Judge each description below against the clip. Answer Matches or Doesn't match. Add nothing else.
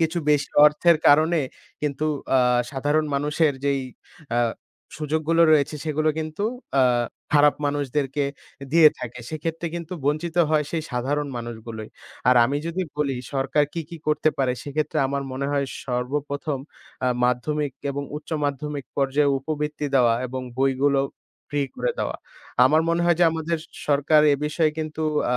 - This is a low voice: Doesn't match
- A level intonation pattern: Matches